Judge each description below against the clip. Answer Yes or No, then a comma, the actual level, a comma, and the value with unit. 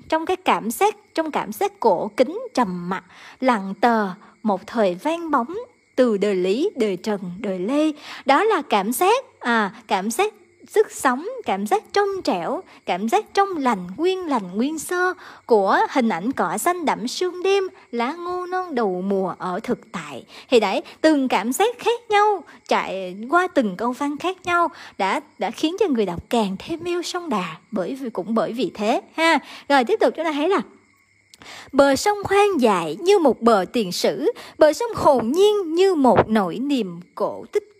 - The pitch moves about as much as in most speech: No, wide, 9.0 semitones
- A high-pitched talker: Yes, very high, 280 Hz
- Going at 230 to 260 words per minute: No, average, 190 wpm